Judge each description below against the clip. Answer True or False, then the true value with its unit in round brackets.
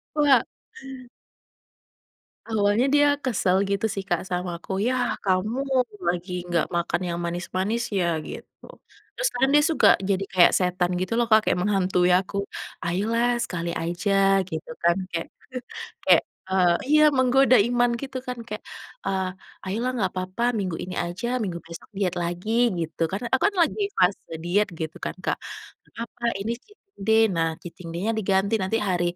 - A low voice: False (195 Hz)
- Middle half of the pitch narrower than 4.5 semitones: False (5.0 semitones)